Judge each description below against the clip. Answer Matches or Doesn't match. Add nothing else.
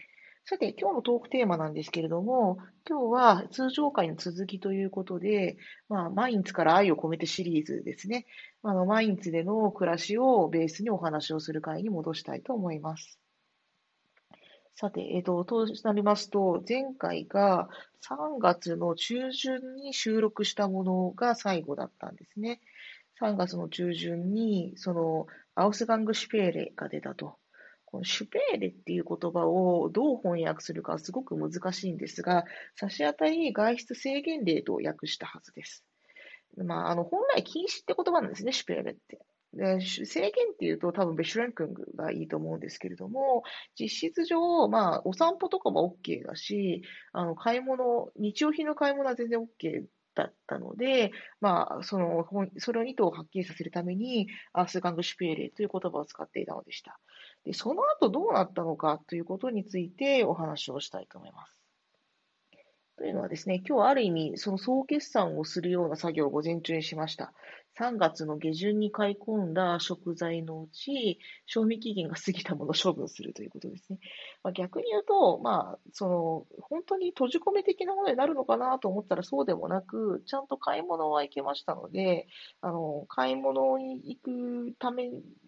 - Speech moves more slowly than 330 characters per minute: Doesn't match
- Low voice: Doesn't match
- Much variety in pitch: Matches